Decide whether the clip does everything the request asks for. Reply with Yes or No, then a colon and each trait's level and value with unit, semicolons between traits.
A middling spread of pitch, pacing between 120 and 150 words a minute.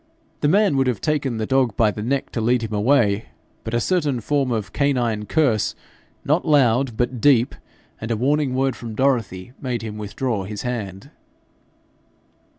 No: average, 4.0 semitones; average, 170 wpm